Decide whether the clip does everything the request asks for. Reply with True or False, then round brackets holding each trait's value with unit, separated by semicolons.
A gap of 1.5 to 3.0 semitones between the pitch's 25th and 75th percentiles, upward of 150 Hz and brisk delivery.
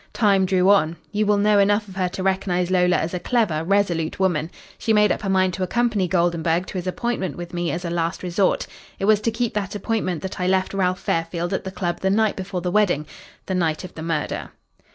True (2.6 semitones; 185 Hz; 235 wpm)